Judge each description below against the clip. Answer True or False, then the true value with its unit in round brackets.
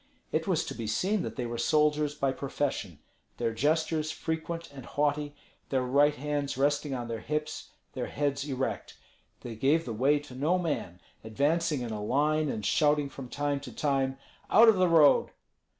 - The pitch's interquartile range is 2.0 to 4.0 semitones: True (2.9 semitones)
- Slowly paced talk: False (180 wpm)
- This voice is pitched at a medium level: True (145 Hz)